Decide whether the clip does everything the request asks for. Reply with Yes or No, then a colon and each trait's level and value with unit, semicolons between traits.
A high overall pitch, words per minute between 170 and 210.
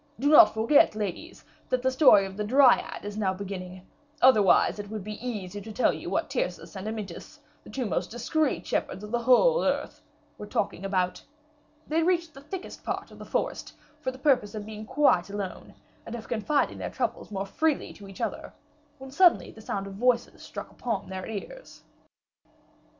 Yes: high, 220 Hz; average, 190 wpm